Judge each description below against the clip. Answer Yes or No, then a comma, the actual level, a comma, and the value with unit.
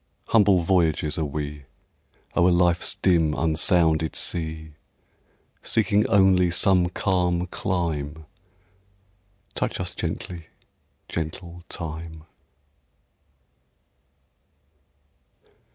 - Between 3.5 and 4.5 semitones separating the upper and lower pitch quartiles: No, narrow, 2.4 semitones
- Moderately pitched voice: No, very low, 85 Hz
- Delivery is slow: Yes, slow, 70 wpm